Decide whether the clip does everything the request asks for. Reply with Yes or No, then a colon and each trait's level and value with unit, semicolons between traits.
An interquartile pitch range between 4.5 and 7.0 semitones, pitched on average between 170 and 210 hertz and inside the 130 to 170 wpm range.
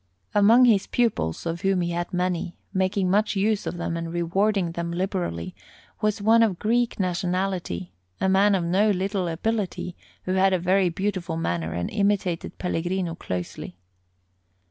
No: average, 2.9 semitones; medium, 185 Hz; average, 155 wpm